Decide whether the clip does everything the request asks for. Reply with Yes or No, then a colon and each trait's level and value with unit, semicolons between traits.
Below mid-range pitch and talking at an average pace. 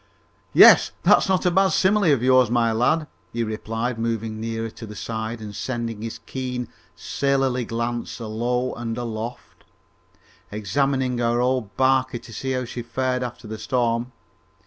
Yes: low, 120 Hz; average, 155 wpm